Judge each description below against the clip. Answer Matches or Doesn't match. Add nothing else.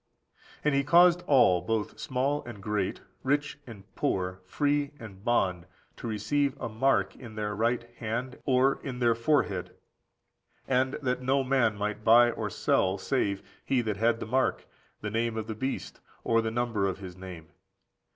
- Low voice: Matches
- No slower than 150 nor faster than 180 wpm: Matches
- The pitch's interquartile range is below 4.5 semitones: Matches